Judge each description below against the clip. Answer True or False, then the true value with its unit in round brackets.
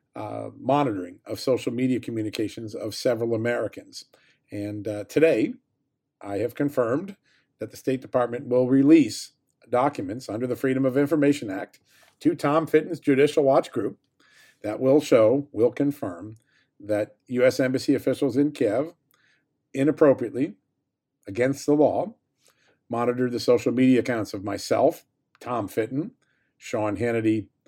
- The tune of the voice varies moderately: True (3.6 semitones)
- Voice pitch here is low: True (130 Hz)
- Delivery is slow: True (130 wpm)